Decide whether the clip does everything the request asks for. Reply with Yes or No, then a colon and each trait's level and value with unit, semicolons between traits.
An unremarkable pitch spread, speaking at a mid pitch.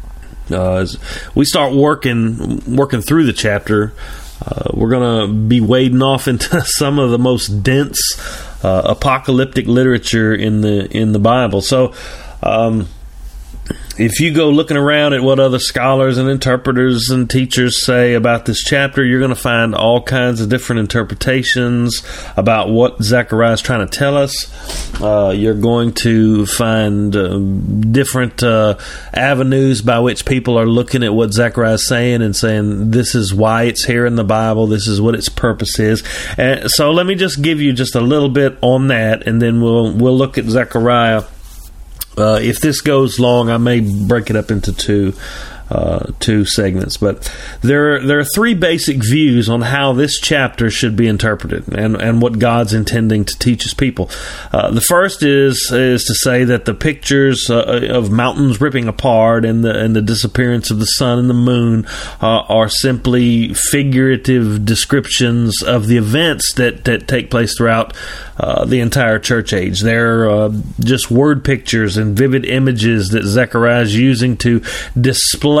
No: average, 3.0 semitones; low, 120 Hz